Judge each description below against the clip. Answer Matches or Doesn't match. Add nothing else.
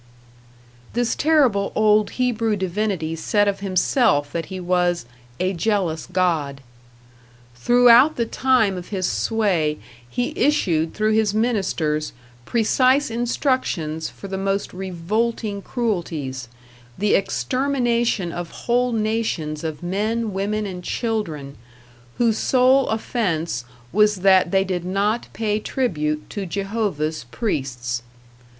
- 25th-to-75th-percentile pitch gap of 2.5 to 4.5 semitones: Doesn't match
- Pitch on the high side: Matches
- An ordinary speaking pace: Doesn't match